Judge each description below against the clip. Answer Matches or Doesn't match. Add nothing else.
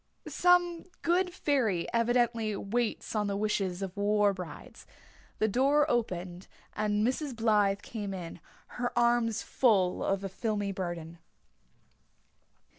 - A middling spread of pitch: Matches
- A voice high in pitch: Matches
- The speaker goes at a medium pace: Doesn't match